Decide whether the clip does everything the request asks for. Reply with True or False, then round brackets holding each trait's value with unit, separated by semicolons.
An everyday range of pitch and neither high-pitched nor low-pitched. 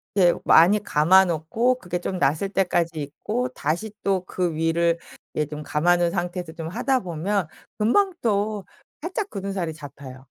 True (4.1 semitones; 175 Hz)